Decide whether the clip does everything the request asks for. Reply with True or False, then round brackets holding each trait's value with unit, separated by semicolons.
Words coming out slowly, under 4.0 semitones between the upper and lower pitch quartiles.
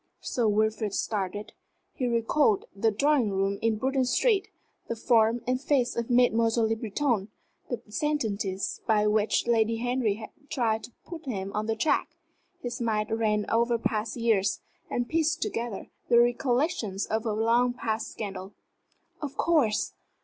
False (150 wpm; 2.6 semitones)